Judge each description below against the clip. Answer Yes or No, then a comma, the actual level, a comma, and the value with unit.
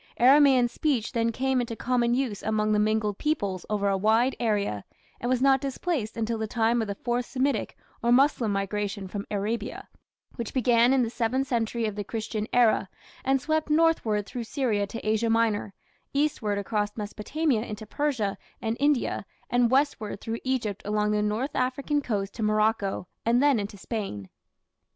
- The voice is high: Yes, high, 230 Hz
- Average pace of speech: Yes, average, 170 wpm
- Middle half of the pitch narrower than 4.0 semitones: Yes, average, 3.5 semitones